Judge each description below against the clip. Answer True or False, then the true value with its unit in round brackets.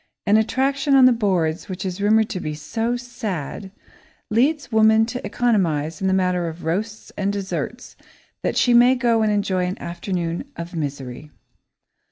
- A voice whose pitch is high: True (200 Hz)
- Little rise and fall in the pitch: False (5.1 semitones)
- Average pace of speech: True (165 wpm)